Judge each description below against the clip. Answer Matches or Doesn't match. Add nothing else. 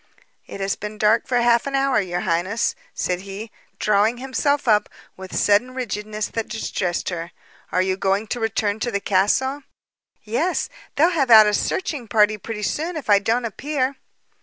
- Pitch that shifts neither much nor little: Matches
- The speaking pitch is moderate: Doesn't match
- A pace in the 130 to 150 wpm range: Doesn't match